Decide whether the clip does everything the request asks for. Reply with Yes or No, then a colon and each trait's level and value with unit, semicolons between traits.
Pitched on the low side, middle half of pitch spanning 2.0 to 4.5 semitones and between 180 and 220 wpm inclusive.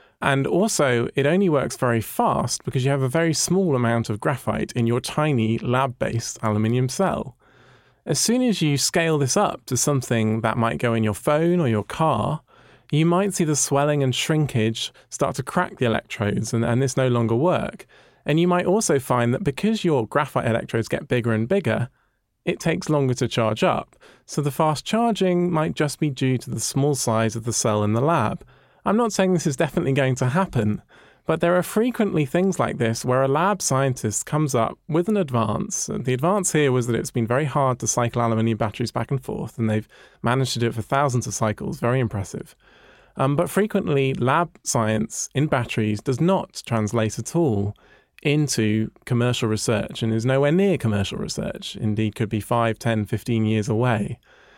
No: low, 130 Hz; average, 5.2 semitones; average, 200 wpm